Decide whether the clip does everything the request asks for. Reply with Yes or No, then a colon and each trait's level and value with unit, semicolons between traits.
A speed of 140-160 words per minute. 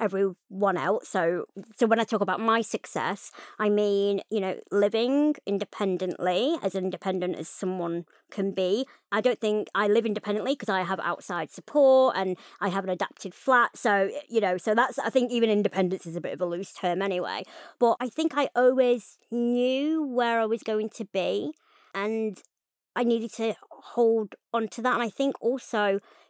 No: average, 185 wpm